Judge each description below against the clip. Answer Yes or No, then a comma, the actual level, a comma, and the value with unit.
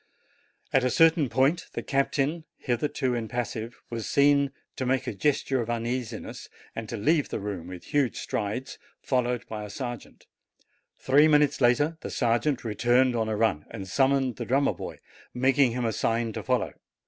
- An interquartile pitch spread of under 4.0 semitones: Yes, average, 3.3 semitones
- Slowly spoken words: No, average, 170 wpm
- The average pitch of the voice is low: Yes, low, 125 Hz